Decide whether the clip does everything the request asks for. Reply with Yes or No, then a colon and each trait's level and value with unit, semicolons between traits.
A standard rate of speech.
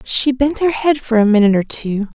No: fast, 245 wpm